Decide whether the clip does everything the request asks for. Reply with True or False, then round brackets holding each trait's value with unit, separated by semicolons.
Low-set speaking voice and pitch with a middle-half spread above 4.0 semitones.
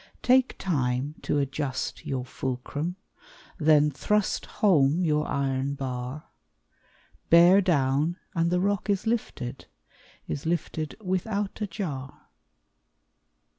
False (155 Hz; 5.3 semitones)